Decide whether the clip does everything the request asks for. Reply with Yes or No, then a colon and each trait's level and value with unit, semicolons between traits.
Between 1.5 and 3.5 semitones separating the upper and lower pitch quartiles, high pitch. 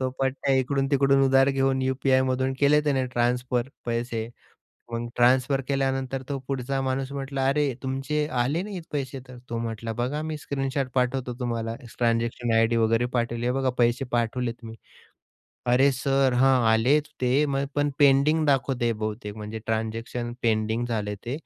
No: narrow, 2.5 semitones; low, 130 Hz